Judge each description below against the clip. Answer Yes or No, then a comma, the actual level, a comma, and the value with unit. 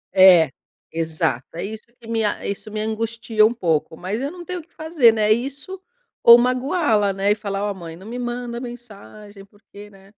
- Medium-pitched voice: No, high, 215 Hz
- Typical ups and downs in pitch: Yes, average, 3.5 semitones